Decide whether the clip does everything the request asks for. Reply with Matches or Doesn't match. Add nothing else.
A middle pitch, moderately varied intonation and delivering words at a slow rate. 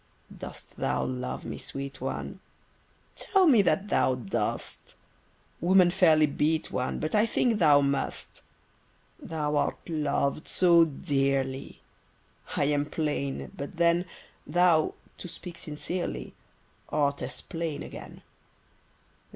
Matches